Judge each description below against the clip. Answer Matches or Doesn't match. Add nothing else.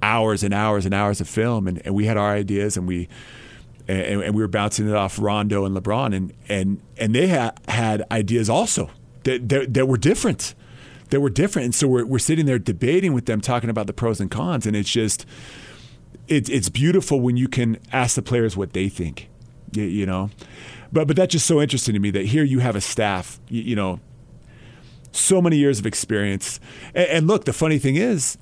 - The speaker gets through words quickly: Matches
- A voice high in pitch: Doesn't match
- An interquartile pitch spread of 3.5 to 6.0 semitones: Matches